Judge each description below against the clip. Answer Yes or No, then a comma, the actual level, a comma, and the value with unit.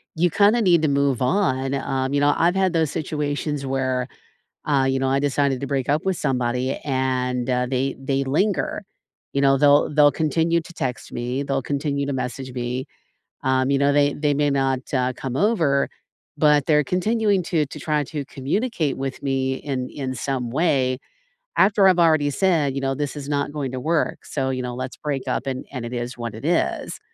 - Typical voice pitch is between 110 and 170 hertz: Yes, medium, 140 Hz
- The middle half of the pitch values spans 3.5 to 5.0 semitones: No, narrow, 2.5 semitones